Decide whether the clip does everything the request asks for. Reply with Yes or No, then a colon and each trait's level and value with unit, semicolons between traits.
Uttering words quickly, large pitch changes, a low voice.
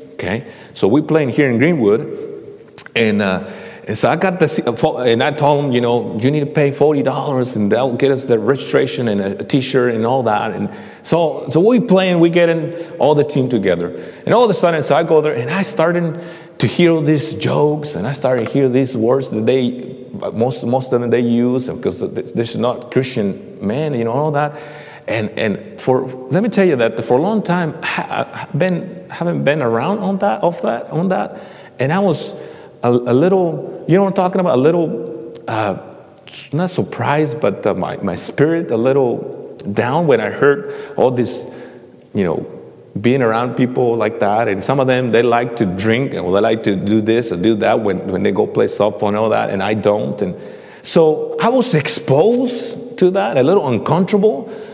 No: fast, 215 wpm; wide, 7.0 semitones; medium, 145 Hz